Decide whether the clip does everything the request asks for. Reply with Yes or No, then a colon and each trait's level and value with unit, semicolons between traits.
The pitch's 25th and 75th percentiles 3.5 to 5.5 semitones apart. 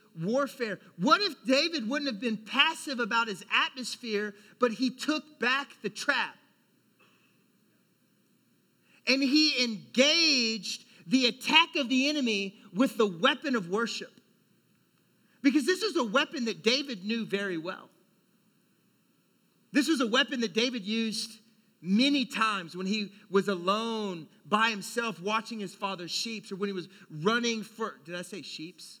Yes: average, 4.4 semitones